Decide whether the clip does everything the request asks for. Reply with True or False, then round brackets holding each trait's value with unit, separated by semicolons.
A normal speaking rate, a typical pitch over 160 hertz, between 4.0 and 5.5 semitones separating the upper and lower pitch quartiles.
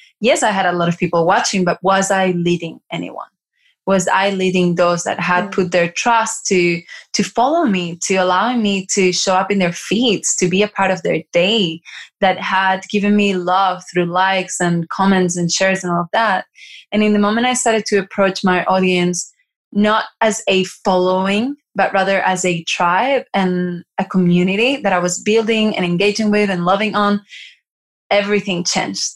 False (185 wpm; 190 Hz; 2.4 semitones)